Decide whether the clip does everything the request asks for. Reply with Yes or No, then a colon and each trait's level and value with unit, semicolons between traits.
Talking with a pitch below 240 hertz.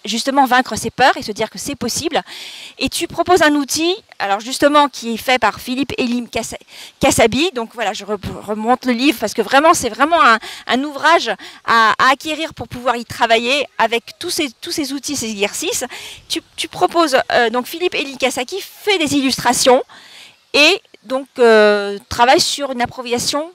No: very high, 260 Hz